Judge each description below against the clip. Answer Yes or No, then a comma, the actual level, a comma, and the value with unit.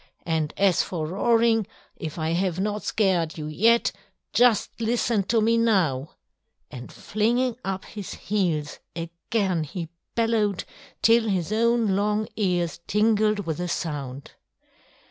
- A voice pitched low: No, high, 200 Hz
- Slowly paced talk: Yes, slow, 130 wpm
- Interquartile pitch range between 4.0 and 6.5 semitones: Yes, average, 5.0 semitones